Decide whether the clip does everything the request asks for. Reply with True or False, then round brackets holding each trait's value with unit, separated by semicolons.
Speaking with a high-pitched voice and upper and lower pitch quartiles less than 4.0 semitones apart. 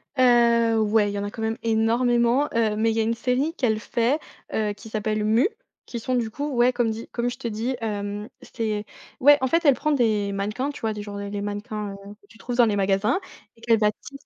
True (225 Hz; 2.6 semitones)